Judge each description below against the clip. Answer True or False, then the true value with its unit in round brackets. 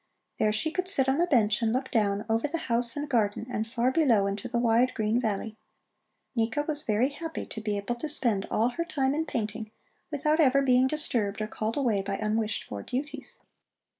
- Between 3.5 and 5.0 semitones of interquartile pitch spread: True (4.6 semitones)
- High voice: True (235 Hz)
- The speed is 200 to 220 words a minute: True (205 wpm)